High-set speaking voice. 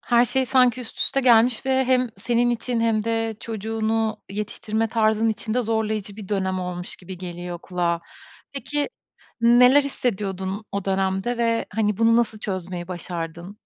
Yes: high, 220 Hz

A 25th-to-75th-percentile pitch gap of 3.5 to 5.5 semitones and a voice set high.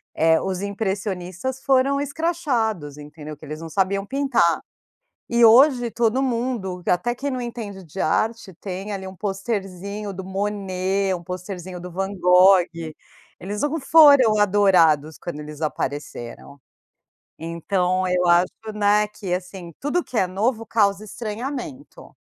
Yes: average, 4.4 semitones; high, 195 Hz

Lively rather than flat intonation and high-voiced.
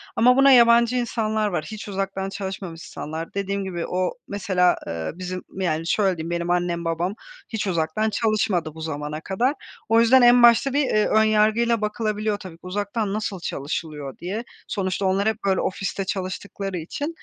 No: average, 3.7 semitones; high, 195 Hz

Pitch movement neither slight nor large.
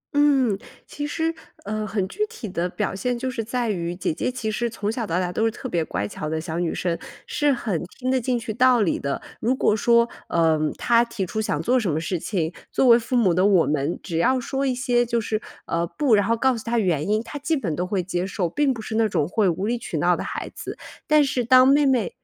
No: wide, 5.8 semitones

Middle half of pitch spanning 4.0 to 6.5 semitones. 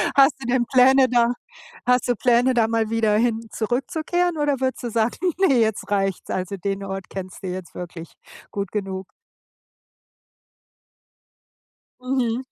Yes: average, 4.4 semitones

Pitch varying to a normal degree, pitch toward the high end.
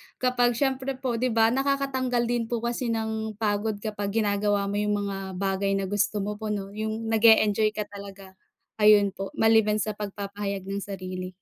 No: narrow, 2.3 semitones; high, 210 Hz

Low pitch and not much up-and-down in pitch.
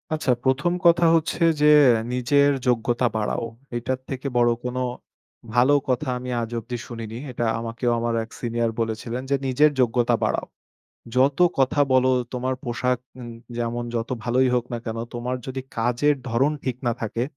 Yes: low, 125 Hz; narrow, 2.0 semitones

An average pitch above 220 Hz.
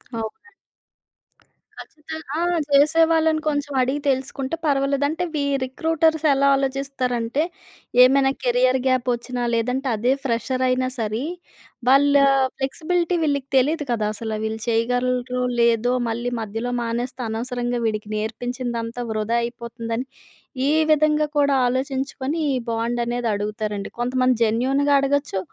Yes: very high, 255 Hz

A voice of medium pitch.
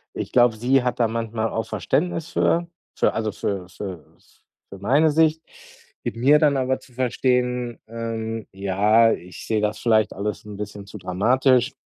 No: low, 115 Hz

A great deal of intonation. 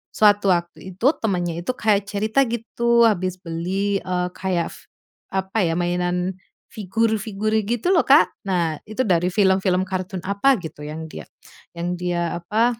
No: average, 3.5 semitones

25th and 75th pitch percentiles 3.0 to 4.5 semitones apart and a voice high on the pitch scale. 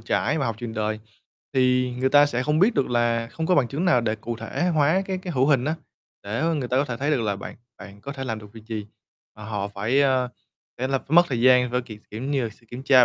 No: average, 3.9 semitones; low, 125 Hz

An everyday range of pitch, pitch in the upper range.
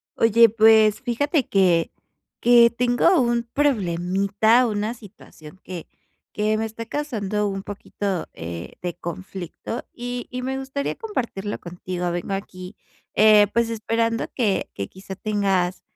Yes: average, 3.9 semitones; high, 215 Hz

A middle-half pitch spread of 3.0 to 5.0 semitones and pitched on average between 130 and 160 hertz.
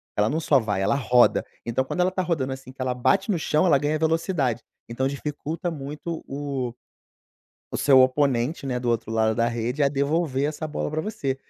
Yes: average, 3.9 semitones; medium, 140 Hz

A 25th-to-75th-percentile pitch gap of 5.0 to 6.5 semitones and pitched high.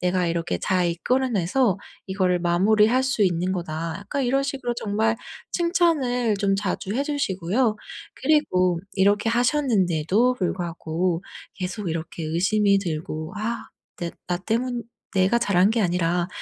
Yes: wide, 5.4 semitones; high, 195 Hz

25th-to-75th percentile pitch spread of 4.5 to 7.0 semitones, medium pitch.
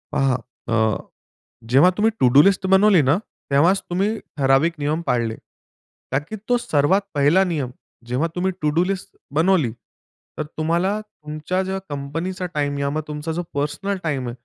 Yes: average, 5.0 semitones; medium, 155 Hz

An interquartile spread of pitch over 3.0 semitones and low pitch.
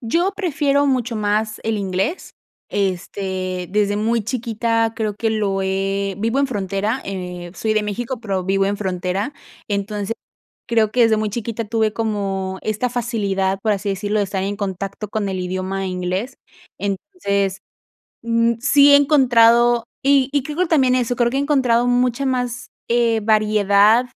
No: average, 3.6 semitones; high, 215 Hz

